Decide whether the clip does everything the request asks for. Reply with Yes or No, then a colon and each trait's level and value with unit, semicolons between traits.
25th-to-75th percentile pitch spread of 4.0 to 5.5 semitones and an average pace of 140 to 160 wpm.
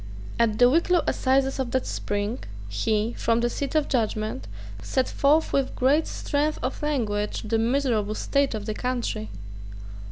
Yes: average, 4.4 semitones; average, 155 wpm